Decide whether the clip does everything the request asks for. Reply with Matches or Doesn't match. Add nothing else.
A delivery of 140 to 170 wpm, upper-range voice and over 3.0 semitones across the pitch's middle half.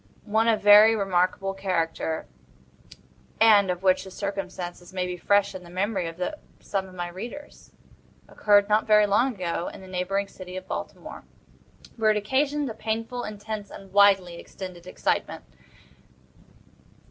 Doesn't match